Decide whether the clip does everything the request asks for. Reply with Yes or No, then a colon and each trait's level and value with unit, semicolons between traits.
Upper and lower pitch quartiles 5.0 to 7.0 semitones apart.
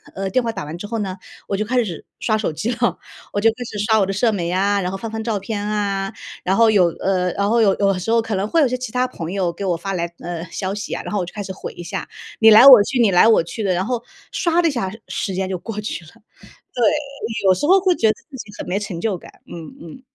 No: average, 3.3 semitones